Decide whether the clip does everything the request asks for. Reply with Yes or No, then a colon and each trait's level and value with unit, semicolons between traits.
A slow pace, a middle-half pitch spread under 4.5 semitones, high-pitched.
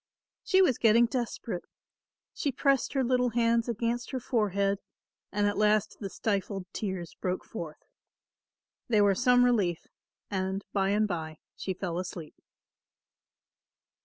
Yes: slow, 130 wpm; average, 4.0 semitones; high, 210 Hz